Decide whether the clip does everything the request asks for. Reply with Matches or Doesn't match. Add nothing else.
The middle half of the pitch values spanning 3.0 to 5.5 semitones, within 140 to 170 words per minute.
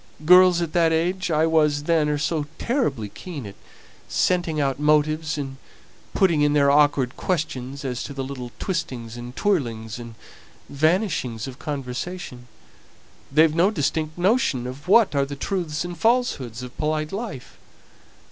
Matches